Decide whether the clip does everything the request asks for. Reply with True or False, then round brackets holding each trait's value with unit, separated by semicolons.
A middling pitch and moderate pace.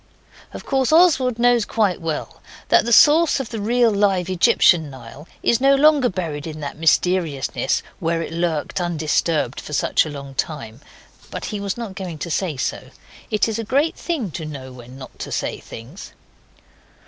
True (180 Hz; 180 wpm)